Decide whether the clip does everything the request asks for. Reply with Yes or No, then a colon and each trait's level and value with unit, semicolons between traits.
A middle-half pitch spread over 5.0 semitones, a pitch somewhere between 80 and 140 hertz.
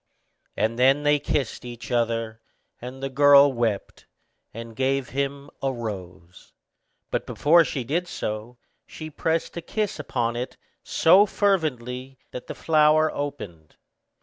No: average, 4.1 semitones; low, 135 Hz